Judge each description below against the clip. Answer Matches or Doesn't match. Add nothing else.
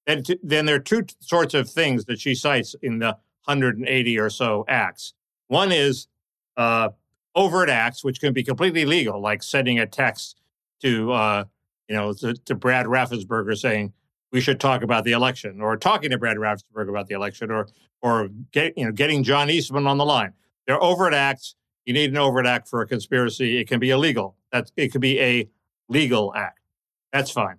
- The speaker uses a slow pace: Doesn't match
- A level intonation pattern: Doesn't match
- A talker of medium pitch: Doesn't match